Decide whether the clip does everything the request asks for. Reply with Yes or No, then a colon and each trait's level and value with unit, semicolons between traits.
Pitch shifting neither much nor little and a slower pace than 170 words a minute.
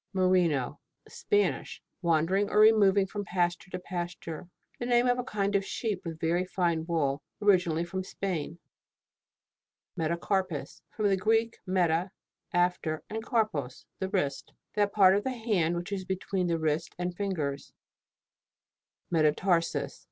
Yes: average, 3.3 semitones; slow, 135 wpm